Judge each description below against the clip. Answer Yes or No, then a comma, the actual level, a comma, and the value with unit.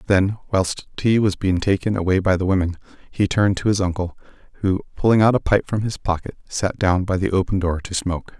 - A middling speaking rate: No, fast, 220 wpm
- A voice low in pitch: Yes, very low, 95 Hz